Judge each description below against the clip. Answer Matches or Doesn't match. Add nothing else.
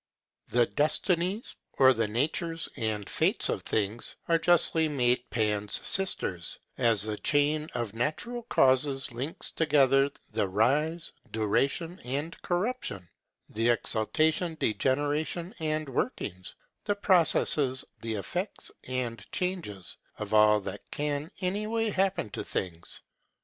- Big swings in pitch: Matches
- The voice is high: Doesn't match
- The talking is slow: Matches